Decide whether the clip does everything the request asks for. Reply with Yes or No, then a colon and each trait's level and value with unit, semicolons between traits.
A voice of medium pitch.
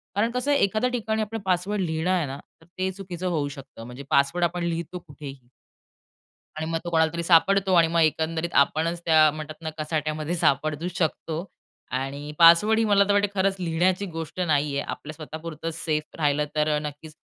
Yes: medium, 165 Hz